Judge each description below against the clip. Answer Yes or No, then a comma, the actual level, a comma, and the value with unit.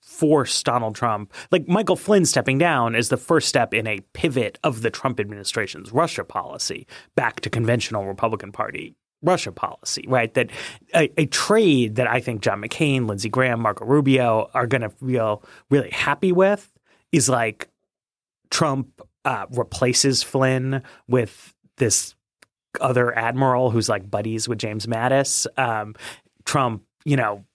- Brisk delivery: No, average, 150 wpm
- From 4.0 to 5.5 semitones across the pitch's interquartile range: No, average, 3.3 semitones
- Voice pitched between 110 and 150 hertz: Yes, low, 125 Hz